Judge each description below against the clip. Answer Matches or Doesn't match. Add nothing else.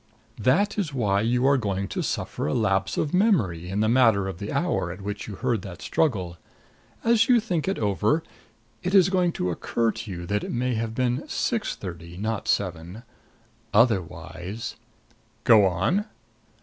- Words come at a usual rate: Matches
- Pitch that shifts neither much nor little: Doesn't match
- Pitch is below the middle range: Matches